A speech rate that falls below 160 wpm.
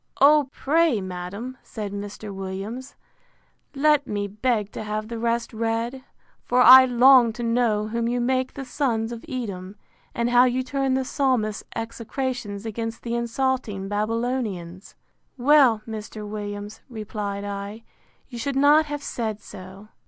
Yes: average, 145 wpm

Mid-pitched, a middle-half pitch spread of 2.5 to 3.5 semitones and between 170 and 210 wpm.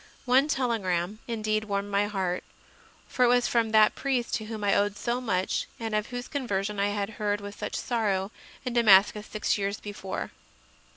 No: high, 210 Hz; average, 2.8 semitones; average, 180 wpm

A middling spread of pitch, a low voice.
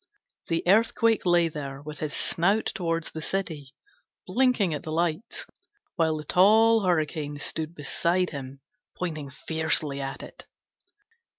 No: average, 3.5 semitones; medium, 165 Hz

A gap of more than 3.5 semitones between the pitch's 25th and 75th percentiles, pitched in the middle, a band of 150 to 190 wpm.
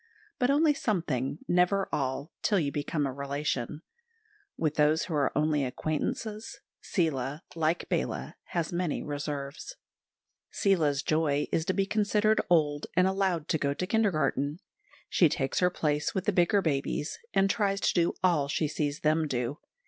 Yes: average, 4.5 semitones; medium, 155 Hz; average, 160 wpm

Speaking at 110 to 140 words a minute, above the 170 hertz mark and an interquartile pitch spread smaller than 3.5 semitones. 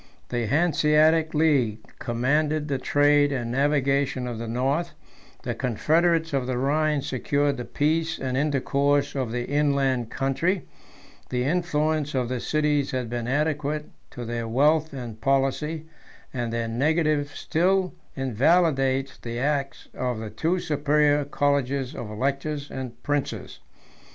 No: slow, 135 wpm; medium, 140 Hz; average, 3.1 semitones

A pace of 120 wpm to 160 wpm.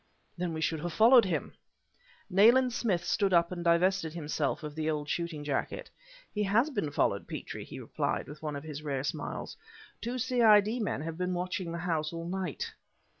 No: average, 185 wpm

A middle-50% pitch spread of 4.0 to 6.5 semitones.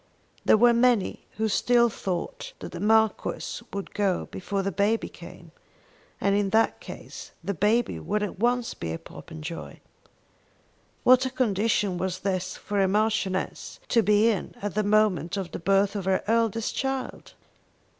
No: average, 3.0 semitones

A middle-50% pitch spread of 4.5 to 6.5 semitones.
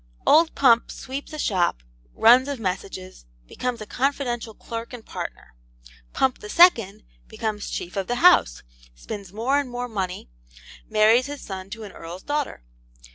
Yes: average, 5.2 semitones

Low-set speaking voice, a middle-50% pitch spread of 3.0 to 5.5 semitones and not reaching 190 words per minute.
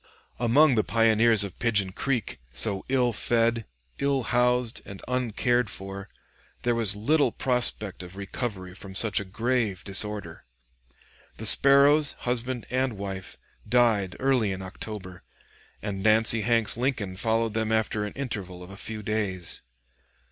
Yes: low, 110 Hz; average, 3.8 semitones; average, 140 wpm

